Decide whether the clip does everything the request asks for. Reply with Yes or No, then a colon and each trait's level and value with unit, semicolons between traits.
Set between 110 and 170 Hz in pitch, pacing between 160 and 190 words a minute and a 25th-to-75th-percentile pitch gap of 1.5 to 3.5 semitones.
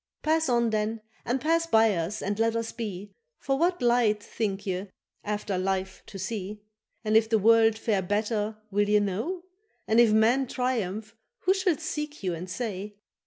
No: high, 220 Hz; average, 175 wpm; average, 2.9 semitones